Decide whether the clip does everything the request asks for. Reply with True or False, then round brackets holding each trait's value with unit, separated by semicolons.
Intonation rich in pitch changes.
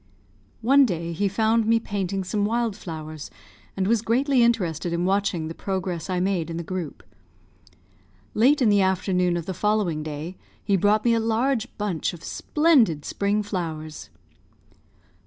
False (4.5 semitones)